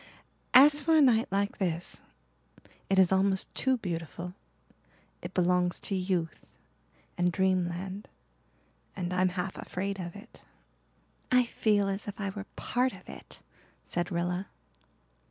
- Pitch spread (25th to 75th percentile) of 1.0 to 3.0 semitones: Yes, narrow, 2.5 semitones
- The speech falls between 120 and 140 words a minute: Yes, slow, 135 wpm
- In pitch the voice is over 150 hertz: Yes, high, 190 Hz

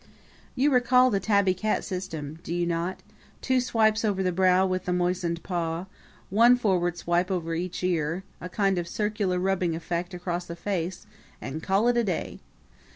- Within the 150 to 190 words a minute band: Yes, average, 175 wpm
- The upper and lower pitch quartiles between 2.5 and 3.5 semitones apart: Yes, average, 3.0 semitones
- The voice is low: No, medium, 185 Hz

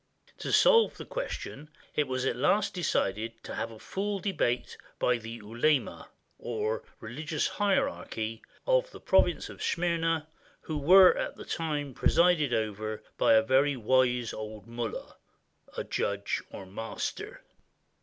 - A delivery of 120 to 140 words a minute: Yes, slow, 135 wpm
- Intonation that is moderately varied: No, wide, 6.7 semitones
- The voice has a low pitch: Yes, low, 130 Hz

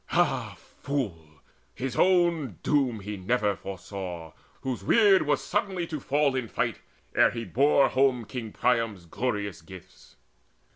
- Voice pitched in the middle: No, low, 125 Hz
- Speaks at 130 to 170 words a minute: Yes, slow, 135 wpm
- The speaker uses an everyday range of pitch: No, wide, 6.3 semitones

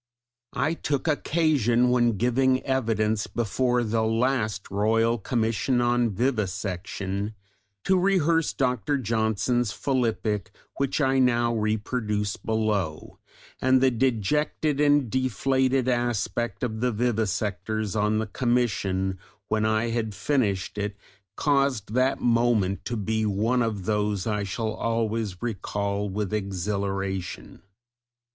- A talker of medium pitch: No, low, 115 Hz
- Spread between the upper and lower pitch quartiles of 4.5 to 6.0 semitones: No, average, 3.4 semitones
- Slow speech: Yes, slow, 115 wpm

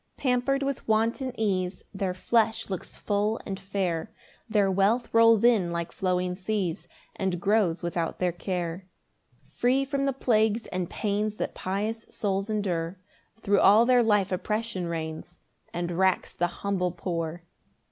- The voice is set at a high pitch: Yes, high, 195 Hz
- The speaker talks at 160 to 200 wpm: No, average, 150 wpm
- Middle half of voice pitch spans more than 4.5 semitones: No, average, 3.8 semitones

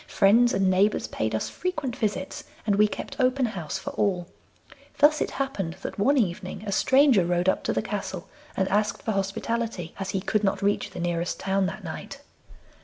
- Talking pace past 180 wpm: Yes, average, 190 wpm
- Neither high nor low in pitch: No, high, 200 Hz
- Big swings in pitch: No, average, 3.8 semitones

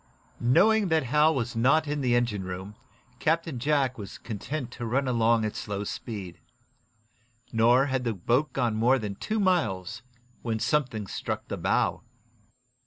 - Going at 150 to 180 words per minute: Yes, average, 155 wpm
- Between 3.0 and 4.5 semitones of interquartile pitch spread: No, average, 5.1 semitones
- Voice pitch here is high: No, low, 120 Hz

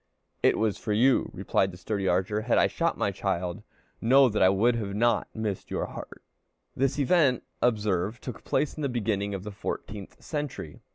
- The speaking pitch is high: No, low, 105 Hz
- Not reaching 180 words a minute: No, average, 185 wpm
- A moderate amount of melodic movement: Yes, average, 4.1 semitones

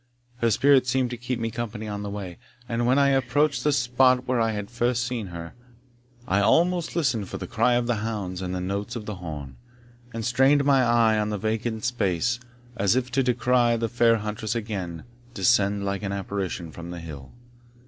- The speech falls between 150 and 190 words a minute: No, average, 200 wpm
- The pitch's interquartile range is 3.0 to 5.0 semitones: Yes, average, 3.8 semitones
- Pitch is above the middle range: No, low, 115 Hz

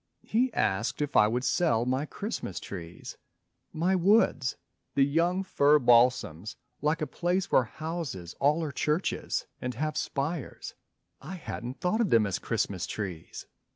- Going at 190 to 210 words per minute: No, average, 150 wpm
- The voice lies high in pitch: No, medium, 140 Hz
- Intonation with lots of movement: Yes, wide, 6.6 semitones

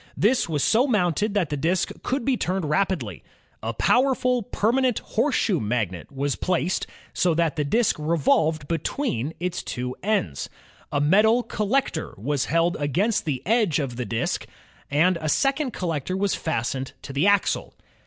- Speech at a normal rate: Yes, average, 160 wpm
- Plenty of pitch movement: Yes, wide, 7.0 semitones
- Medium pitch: Yes, medium, 170 Hz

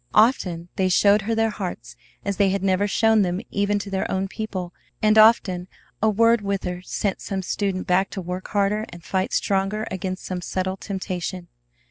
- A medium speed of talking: Yes, average, 185 wpm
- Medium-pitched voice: No, high, 195 Hz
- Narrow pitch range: Yes, narrow, 2.1 semitones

